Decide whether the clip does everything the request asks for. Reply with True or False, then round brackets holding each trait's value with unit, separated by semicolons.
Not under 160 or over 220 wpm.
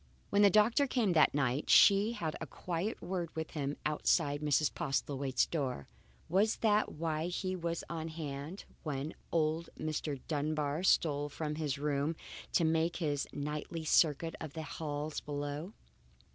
False (150 wpm)